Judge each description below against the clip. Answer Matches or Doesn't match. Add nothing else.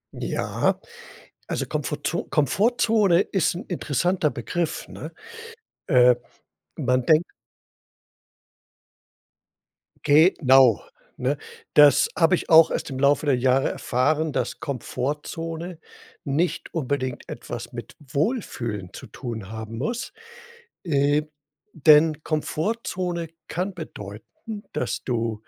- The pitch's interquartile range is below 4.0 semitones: Doesn't match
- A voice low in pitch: Doesn't match